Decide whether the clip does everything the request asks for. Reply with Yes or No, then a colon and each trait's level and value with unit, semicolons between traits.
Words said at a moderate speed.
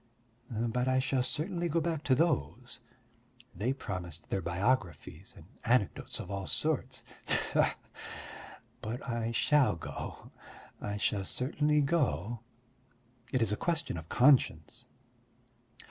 No: slow, 120 wpm